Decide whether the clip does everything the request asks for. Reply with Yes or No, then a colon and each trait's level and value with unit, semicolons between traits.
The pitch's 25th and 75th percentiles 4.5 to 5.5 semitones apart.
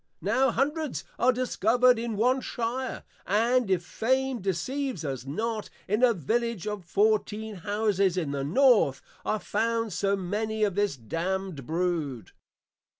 Yes: average, 4.9 semitones